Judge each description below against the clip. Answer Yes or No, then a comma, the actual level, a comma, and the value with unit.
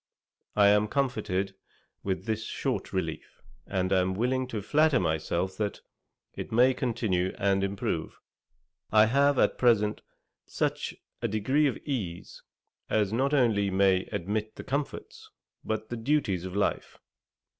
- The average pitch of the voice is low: Yes, low, 105 Hz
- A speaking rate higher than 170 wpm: No, average, 140 wpm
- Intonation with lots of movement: No, average, 4.5 semitones